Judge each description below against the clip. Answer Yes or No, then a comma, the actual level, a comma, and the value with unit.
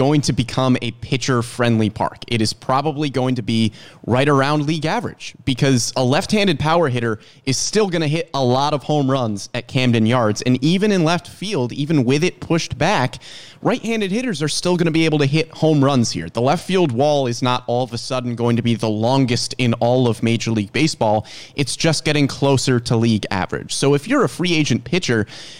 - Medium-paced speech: No, fast, 225 wpm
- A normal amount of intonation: Yes, average, 4.6 semitones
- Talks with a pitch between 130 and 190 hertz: Yes, low, 135 Hz